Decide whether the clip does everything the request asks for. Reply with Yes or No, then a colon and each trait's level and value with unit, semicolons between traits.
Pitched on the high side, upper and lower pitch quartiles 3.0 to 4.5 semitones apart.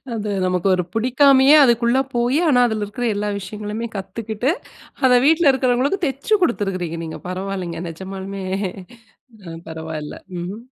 No: high, 215 Hz; average, 5.2 semitones